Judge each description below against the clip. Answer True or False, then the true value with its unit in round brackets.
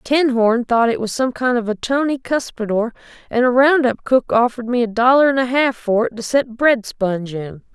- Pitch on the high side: True (240 Hz)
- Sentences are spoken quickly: True (225 wpm)